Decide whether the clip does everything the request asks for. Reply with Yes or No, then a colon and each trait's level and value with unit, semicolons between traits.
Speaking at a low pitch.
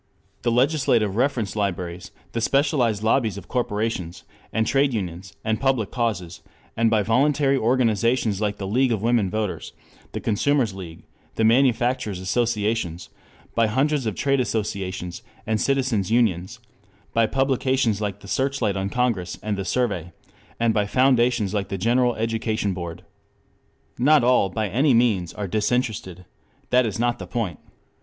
Yes: low, 110 Hz